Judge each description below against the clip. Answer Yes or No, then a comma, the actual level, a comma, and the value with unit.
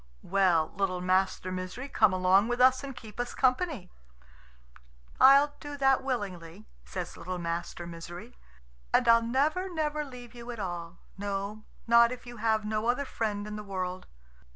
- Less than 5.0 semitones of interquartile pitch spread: No, average, 5.3 semitones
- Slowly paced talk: No, average, 160 wpm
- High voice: Yes, high, 215 Hz